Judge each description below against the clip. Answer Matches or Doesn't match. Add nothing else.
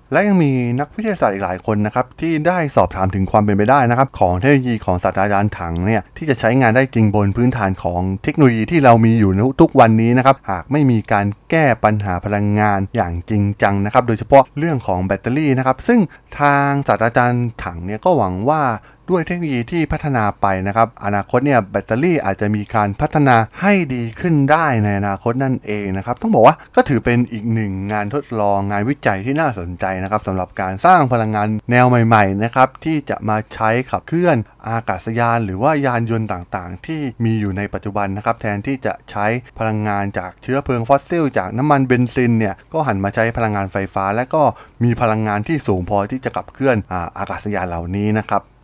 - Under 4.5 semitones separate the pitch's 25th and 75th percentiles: Doesn't match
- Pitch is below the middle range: Matches